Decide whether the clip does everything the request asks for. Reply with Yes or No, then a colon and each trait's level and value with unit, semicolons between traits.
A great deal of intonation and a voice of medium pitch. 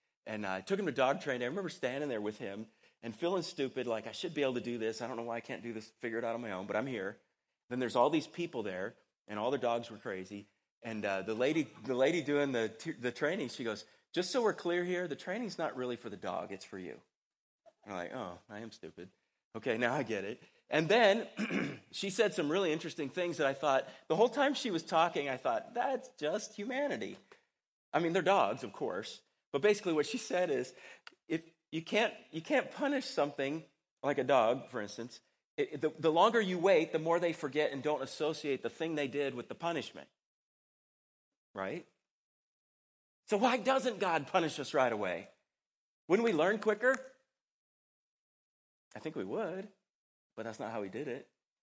Yes: wide, 8.7 semitones; medium, 155 Hz